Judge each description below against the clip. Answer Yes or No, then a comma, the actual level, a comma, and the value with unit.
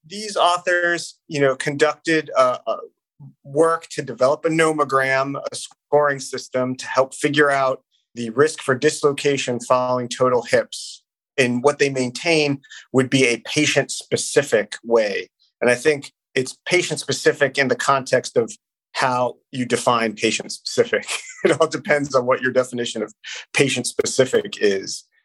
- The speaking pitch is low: No, medium, 145 Hz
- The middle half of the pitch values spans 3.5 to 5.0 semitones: Yes, average, 4.0 semitones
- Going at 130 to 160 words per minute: Yes, average, 145 wpm